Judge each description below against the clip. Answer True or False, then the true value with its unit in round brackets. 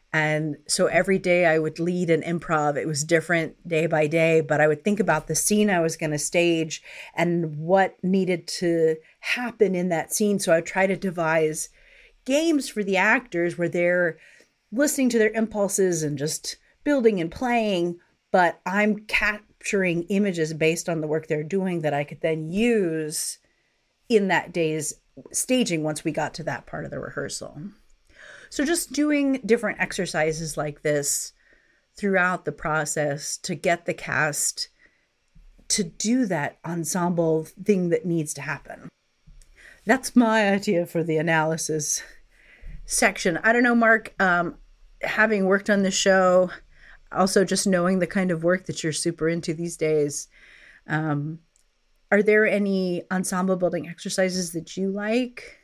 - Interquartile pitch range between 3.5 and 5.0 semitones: True (4.3 semitones)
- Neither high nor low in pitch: True (175 Hz)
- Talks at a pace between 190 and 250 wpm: False (160 wpm)